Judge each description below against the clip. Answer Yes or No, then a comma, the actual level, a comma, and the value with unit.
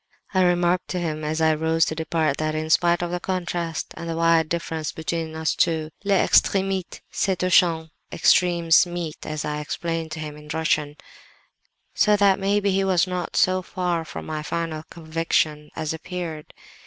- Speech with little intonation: Yes, narrow, 2.2 semitones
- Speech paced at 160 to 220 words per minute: Yes, average, 175 wpm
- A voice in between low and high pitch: Yes, medium, 165 Hz